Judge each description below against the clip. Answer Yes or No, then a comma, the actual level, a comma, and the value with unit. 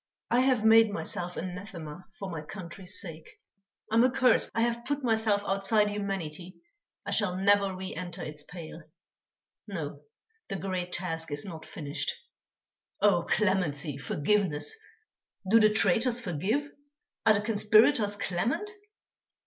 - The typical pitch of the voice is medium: No, high, 195 Hz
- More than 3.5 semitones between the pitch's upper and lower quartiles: Yes, average, 4.2 semitones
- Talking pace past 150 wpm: No, slow, 135 wpm